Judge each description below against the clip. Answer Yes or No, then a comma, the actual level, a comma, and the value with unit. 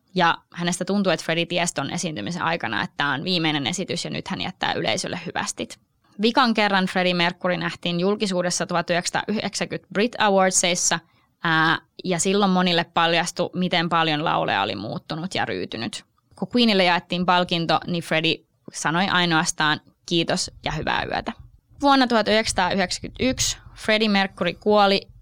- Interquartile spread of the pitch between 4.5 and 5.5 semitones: No, average, 2.7 semitones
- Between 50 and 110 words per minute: No, average, 135 wpm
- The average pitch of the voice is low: No, medium, 175 Hz